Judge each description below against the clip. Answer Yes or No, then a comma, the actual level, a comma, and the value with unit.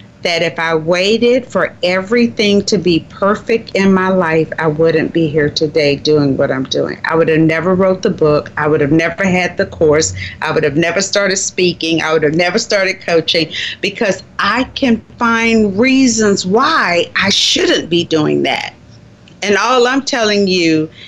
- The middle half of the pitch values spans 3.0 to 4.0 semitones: No, average, 4.4 semitones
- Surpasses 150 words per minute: Yes, average, 180 wpm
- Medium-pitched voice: Yes, medium, 180 Hz